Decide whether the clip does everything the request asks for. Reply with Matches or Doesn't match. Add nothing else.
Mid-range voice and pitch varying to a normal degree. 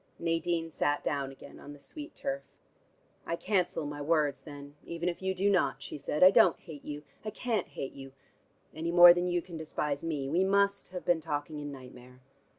Matches